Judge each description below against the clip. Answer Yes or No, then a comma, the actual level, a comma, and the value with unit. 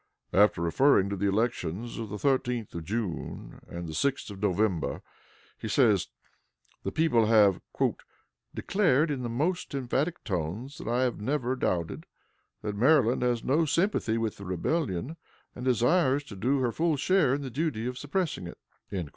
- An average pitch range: No, wide, 5.7 semitones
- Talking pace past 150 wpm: Yes, average, 165 wpm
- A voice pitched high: No, low, 120 Hz